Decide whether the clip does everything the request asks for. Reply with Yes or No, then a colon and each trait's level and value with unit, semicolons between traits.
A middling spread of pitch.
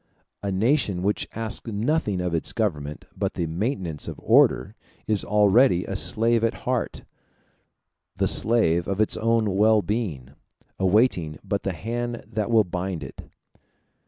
Yes: average, 4.2 semitones